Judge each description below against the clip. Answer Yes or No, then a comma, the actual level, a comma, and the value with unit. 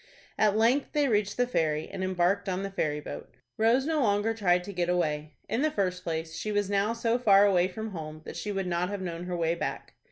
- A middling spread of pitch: Yes, average, 3.8 semitones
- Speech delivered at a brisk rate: Yes, fast, 235 wpm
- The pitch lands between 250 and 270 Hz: No, high, 195 Hz